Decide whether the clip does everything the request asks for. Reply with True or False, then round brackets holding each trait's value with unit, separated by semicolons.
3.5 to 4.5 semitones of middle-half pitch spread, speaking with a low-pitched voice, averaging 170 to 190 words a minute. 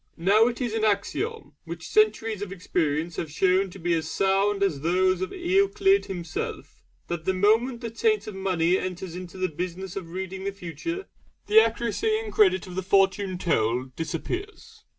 False (4.2 semitones; 190 Hz; 175 wpm)